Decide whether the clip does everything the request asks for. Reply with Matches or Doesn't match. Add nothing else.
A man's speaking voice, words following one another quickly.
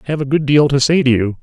Matches